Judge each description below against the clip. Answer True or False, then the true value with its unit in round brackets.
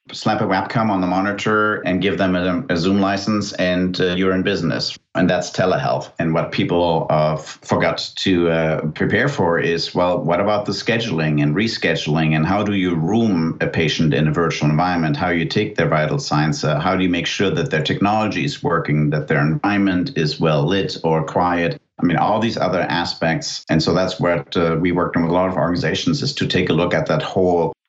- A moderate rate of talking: False (220 wpm)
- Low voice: True (90 Hz)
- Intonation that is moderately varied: True (3.6 semitones)